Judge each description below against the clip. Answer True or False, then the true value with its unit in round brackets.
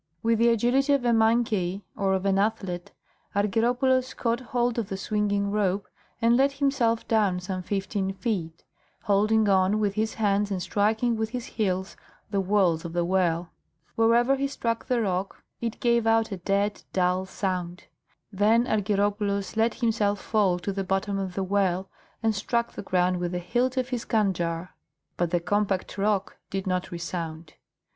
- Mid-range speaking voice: False (205 Hz)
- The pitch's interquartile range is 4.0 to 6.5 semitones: False (3.4 semitones)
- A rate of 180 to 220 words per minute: False (170 wpm)